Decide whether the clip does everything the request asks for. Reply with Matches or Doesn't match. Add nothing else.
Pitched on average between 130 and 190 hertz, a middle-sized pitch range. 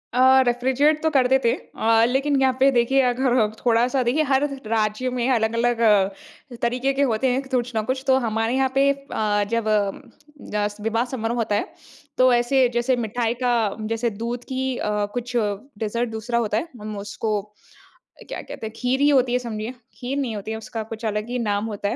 Doesn't match